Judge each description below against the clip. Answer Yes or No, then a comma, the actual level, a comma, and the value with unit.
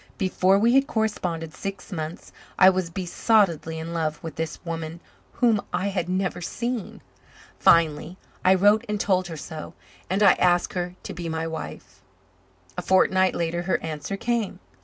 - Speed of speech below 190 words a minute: Yes, average, 160 wpm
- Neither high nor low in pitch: Yes, medium, 180 Hz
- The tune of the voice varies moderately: Yes, average, 3.3 semitones